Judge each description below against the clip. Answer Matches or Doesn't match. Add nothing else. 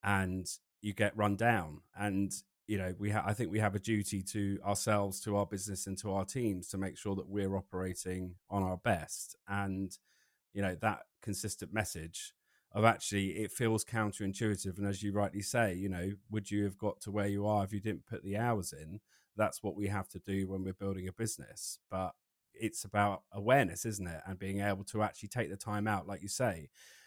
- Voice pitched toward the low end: Matches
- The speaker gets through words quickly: Matches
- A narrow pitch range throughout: Matches